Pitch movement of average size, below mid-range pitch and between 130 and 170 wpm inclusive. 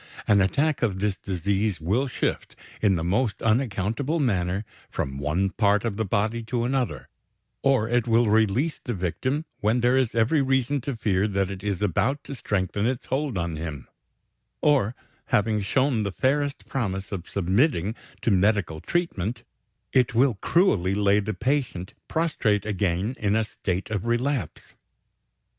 Yes: average, 4.9 semitones; low, 110 Hz; average, 155 wpm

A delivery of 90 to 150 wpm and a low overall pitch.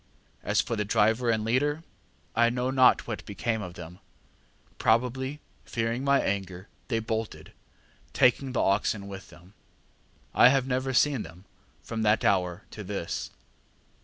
Yes: average, 145 wpm; low, 115 Hz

